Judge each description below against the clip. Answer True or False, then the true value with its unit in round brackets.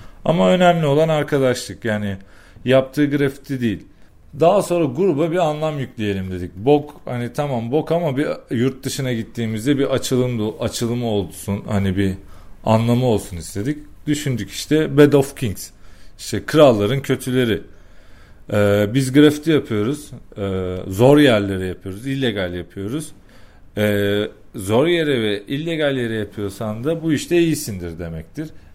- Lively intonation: True (6.5 semitones)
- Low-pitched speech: True (120 Hz)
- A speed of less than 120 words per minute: False (130 wpm)